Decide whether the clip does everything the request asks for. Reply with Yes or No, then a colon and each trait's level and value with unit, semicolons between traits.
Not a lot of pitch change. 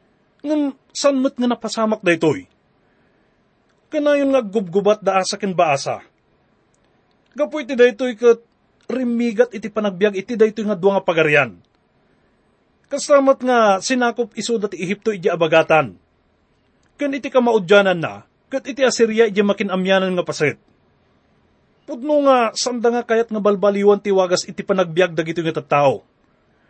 No: average, 4.8 semitones